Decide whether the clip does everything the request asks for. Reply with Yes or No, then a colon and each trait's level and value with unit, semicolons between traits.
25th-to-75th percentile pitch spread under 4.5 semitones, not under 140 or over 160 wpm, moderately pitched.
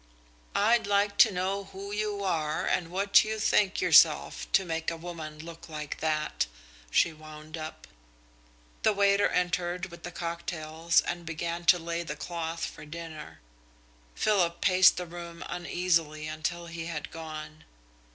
Yes: average, 2.8 semitones; average, 150 wpm; medium, 170 Hz